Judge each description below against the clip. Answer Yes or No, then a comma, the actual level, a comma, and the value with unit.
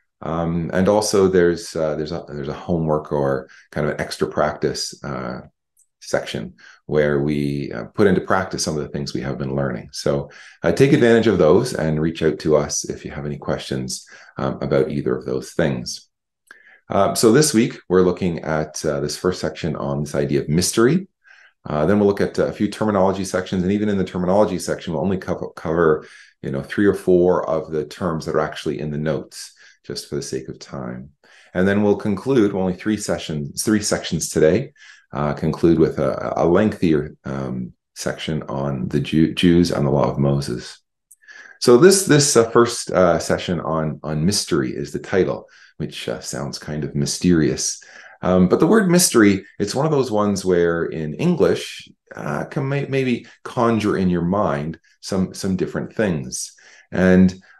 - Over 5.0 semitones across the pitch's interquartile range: Yes, wide, 5.6 semitones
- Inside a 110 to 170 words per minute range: No, average, 190 wpm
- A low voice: Yes, very low, 85 Hz